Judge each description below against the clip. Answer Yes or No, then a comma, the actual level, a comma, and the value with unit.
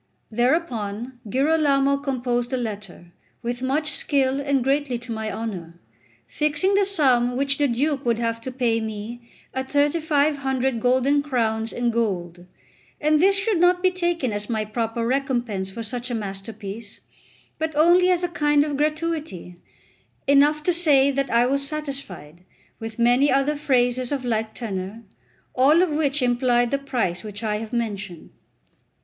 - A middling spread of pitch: Yes, average, 4.4 semitones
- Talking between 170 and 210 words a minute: No, average, 155 wpm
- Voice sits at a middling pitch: No, very high, 255 Hz